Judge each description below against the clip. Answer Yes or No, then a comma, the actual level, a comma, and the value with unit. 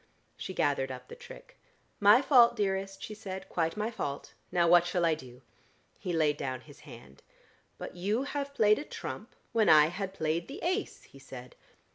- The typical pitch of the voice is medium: Yes, medium, 175 Hz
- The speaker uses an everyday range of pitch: No, wide, 6.5 semitones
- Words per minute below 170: No, average, 185 wpm